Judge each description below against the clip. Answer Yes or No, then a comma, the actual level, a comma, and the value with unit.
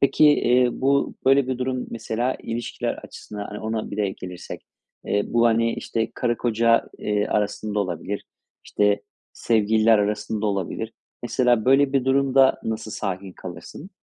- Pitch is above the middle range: No, low, 115 Hz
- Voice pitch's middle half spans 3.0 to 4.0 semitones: Yes, average, 3.5 semitones